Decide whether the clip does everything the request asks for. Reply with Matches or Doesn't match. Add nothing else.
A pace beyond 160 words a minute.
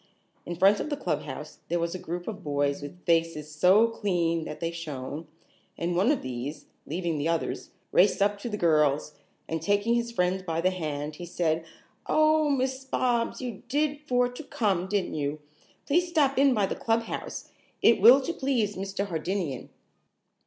Matches